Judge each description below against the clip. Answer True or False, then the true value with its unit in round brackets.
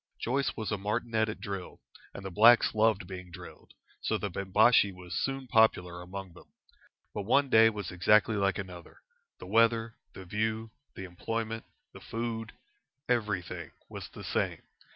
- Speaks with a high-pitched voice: False (105 Hz)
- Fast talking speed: False (155 wpm)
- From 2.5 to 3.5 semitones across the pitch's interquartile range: True (3.1 semitones)